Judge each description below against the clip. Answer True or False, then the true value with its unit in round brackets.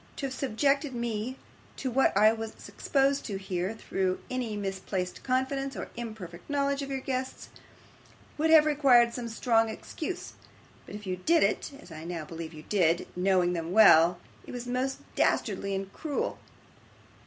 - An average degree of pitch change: False (6.1 semitones)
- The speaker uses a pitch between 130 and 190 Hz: False (225 Hz)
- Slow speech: False (165 wpm)